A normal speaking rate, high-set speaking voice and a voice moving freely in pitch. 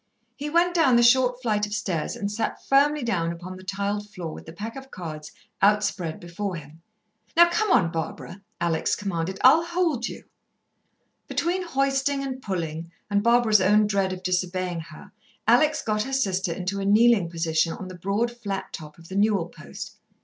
Yes: average, 185 wpm; high, 200 Hz; wide, 5.9 semitones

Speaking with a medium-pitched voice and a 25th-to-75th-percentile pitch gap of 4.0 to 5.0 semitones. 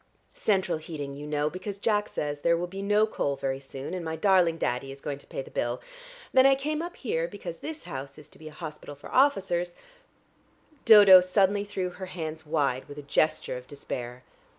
No: medium, 165 Hz; wide, 5.6 semitones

